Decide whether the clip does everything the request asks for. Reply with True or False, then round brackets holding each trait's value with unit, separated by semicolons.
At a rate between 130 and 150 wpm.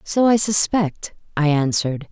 True (140 wpm)